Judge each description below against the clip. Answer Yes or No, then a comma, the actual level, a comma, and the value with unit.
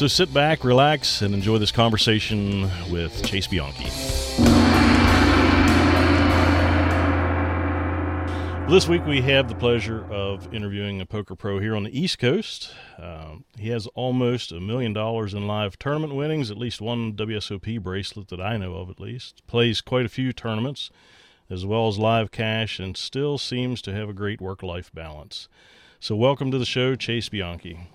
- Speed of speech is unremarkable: Yes, average, 165 wpm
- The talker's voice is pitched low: Yes, low, 105 Hz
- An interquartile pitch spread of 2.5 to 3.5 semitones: No, average, 4.6 semitones